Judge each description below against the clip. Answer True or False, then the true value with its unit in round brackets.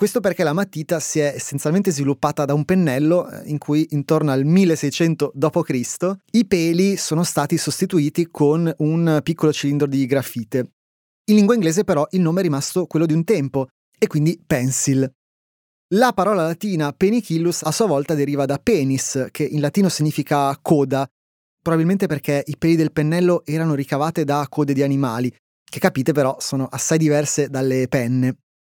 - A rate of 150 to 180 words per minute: True (165 wpm)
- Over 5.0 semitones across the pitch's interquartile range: False (3.5 semitones)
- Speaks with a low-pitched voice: False (155 Hz)